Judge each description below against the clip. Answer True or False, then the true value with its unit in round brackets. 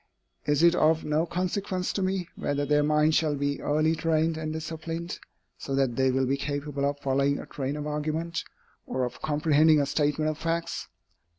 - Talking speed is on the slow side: False (185 wpm)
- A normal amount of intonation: False (2.3 semitones)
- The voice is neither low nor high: True (150 Hz)